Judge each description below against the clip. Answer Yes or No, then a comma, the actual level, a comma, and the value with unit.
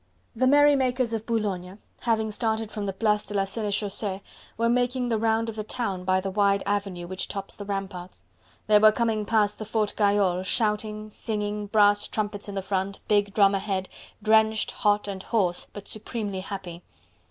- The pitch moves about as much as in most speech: No, narrow, 2.0 semitones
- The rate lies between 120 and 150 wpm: No, average, 175 wpm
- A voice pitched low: No, high, 210 Hz